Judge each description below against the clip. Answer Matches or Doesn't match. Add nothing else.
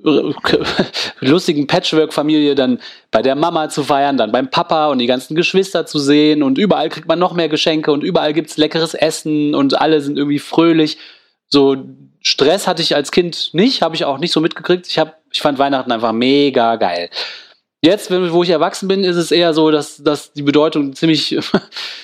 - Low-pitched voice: Doesn't match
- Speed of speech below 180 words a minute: Doesn't match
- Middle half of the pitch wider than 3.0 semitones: Doesn't match